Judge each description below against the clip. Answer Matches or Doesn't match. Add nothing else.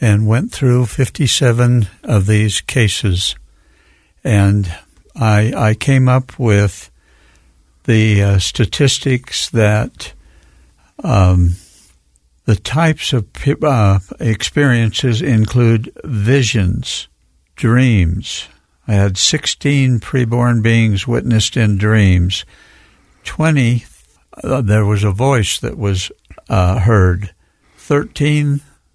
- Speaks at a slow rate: Matches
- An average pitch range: Matches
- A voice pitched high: Doesn't match